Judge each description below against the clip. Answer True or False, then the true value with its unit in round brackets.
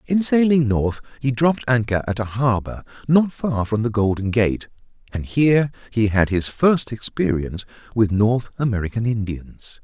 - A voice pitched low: True (115 Hz)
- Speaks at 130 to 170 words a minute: True (160 wpm)